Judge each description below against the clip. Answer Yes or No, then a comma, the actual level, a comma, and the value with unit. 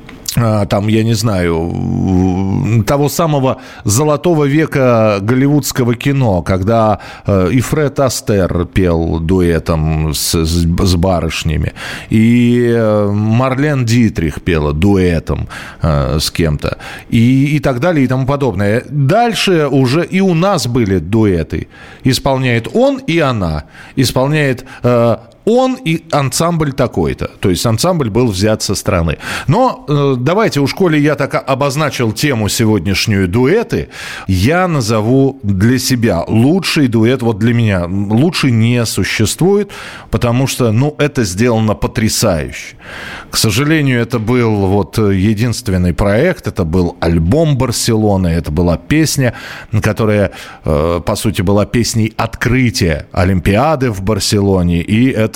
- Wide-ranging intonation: Yes, wide, 5.7 semitones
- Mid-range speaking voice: No, low, 115 Hz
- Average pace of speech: Yes, average, 120 wpm